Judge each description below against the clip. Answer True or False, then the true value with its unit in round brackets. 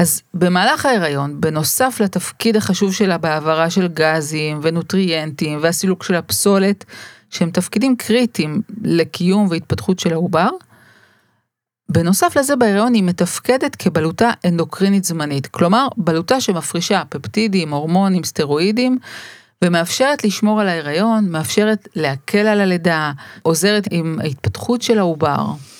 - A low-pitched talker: False (180 Hz)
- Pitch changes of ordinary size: True (4.7 semitones)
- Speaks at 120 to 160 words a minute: False (110 wpm)